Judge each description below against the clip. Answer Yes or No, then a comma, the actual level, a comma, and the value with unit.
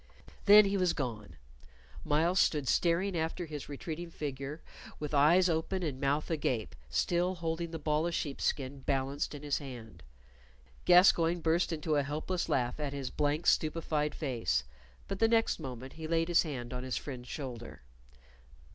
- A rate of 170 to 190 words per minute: No, average, 160 wpm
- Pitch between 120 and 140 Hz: No, medium, 150 Hz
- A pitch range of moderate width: Yes, average, 3.8 semitones